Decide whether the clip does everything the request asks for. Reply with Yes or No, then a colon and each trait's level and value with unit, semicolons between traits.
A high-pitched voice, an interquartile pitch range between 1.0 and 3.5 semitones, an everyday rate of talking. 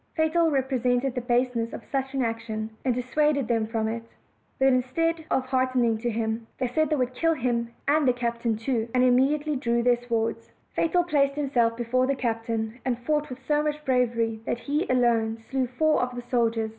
Yes: very high, 250 Hz; average, 2.9 semitones; average, 195 wpm